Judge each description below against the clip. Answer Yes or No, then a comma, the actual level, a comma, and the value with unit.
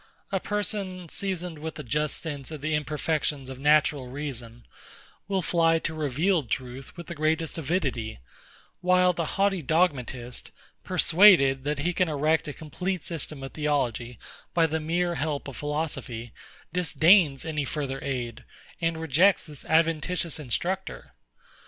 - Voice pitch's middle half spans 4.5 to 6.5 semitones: No, average, 3.8 semitones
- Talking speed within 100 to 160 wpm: Yes, average, 140 wpm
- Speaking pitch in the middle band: Yes, medium, 155 Hz